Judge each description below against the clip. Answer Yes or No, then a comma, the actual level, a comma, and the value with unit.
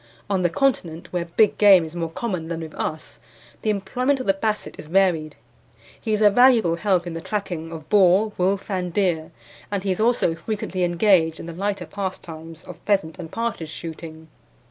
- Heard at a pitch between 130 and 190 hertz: Yes, medium, 185 Hz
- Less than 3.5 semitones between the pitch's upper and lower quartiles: No, average, 3.9 semitones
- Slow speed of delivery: No, average, 190 wpm